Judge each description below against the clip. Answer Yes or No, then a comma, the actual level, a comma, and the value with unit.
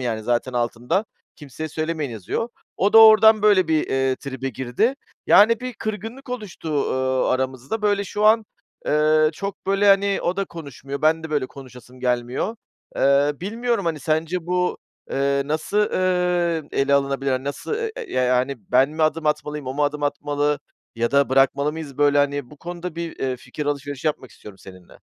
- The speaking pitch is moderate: Yes, medium, 150 Hz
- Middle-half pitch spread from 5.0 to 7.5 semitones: Yes, wide, 5.4 semitones